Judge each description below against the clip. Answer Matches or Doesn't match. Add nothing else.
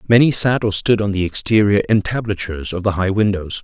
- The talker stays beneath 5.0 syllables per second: Doesn't match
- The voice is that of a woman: Doesn't match